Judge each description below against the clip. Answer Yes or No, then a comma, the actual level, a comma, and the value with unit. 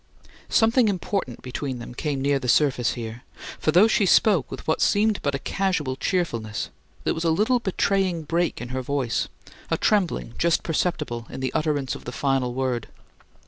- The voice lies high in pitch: No, medium, 145 Hz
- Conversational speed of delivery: Yes, average, 180 wpm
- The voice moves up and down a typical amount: No, wide, 6.3 semitones